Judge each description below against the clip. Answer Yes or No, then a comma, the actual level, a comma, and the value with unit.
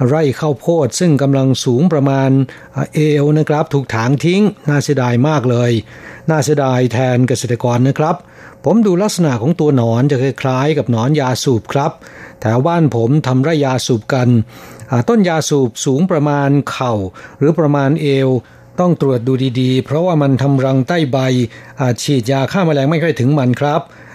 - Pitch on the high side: No, low, 135 Hz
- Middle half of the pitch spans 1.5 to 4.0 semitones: Yes, average, 3.4 semitones